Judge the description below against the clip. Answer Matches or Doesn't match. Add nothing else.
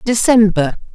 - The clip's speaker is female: Matches